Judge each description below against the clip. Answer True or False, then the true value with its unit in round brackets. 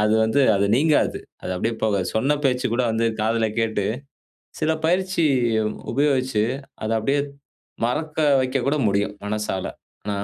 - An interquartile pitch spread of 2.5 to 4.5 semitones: False (4.9 semitones)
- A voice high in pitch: False (115 Hz)